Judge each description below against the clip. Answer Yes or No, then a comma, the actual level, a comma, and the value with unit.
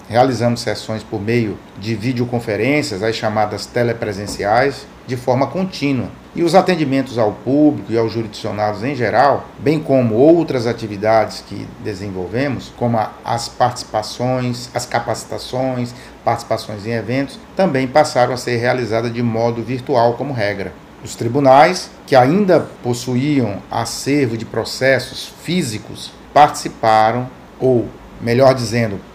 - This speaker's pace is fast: No, slow, 120 wpm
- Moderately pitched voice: No, low, 120 Hz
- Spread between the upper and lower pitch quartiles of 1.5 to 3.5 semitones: Yes, average, 3.1 semitones